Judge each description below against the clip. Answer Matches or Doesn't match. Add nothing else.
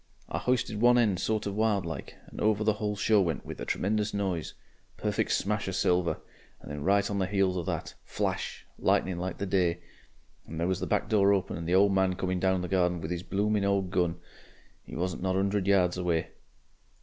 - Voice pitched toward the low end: Matches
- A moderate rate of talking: Doesn't match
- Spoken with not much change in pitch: Matches